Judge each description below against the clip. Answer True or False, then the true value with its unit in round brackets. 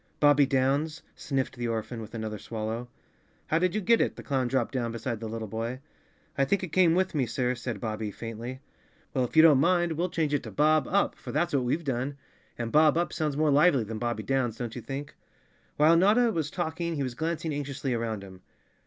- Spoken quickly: True (215 wpm)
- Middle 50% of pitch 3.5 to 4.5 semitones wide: False (5.2 semitones)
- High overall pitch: False (135 Hz)